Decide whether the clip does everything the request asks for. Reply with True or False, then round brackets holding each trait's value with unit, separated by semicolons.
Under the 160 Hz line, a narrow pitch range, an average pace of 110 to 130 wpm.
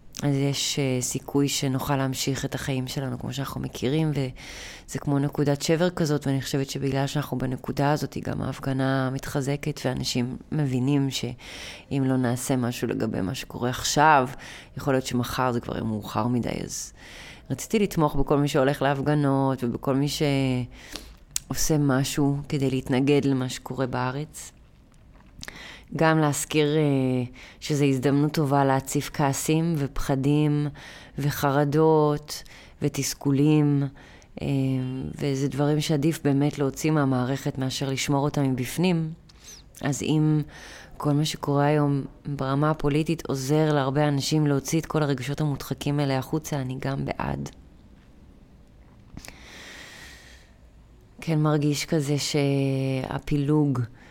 True (140 Hz; 2.1 semitones; 115 wpm)